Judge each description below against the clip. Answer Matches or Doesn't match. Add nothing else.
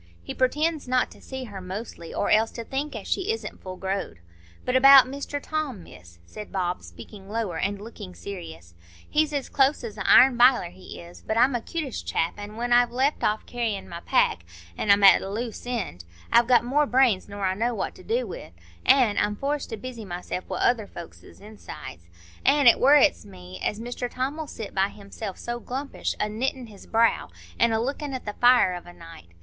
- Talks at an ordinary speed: Doesn't match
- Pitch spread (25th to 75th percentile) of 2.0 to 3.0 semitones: Doesn't match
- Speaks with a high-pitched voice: Matches